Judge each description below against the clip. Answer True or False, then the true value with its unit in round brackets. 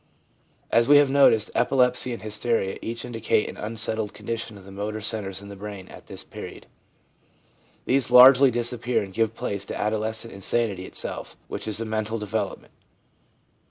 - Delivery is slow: False (165 wpm)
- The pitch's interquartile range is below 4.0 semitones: True (2.6 semitones)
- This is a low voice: True (110 Hz)